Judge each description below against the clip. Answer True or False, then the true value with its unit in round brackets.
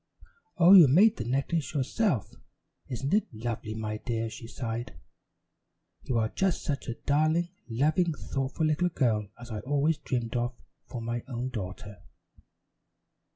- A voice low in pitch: True (125 Hz)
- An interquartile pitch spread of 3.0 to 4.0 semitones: False (5.3 semitones)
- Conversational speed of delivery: True (145 wpm)